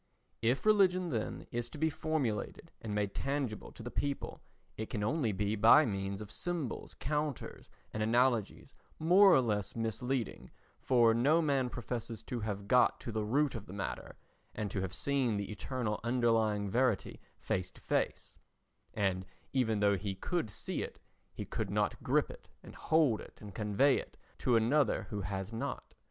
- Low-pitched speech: Yes, low, 115 Hz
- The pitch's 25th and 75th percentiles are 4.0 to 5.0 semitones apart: Yes, average, 4.7 semitones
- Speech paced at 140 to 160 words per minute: No, average, 170 wpm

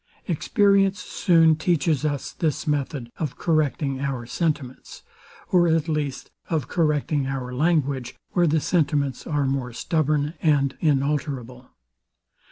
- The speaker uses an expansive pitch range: No, average, 3.1 semitones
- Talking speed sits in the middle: No, slow, 120 wpm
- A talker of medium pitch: Yes, medium, 150 Hz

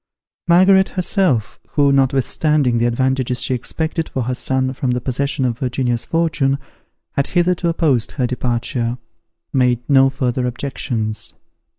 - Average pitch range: Yes, average, 3.3 semitones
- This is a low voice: Yes, low, 130 Hz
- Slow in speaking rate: Yes, slow, 130 wpm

